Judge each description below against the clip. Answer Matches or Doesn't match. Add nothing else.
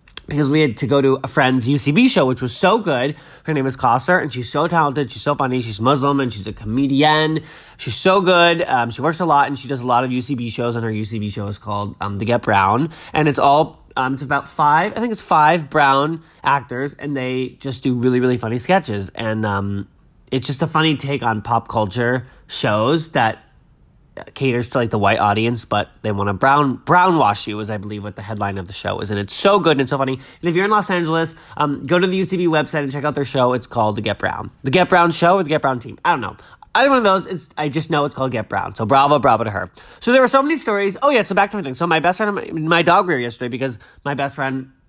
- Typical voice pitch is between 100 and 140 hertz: Matches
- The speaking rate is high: Matches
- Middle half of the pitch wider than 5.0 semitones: Matches